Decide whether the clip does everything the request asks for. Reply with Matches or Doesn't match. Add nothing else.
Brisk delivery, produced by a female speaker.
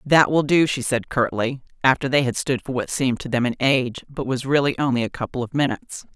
Matches